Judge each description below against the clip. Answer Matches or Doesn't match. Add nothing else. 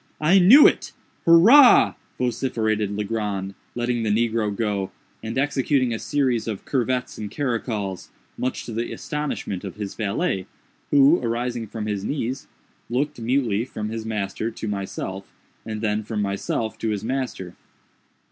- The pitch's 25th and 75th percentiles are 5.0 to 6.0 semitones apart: Doesn't match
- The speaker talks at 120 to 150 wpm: Matches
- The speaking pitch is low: Matches